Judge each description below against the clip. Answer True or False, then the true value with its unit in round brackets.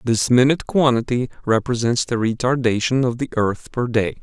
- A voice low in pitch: True (120 Hz)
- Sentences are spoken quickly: False (155 wpm)